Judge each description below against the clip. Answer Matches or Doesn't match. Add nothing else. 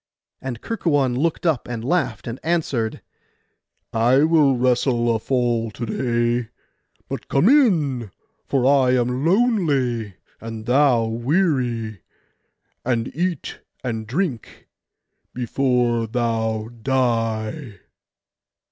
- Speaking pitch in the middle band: Doesn't match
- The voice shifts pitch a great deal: Doesn't match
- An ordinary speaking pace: Doesn't match